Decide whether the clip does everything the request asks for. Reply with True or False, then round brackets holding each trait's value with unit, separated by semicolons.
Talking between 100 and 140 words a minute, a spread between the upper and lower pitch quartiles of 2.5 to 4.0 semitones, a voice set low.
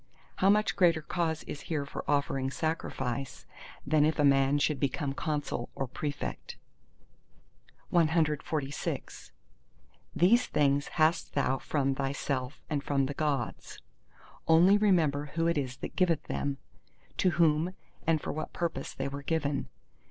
False (135 wpm; 3.0 semitones; 150 Hz)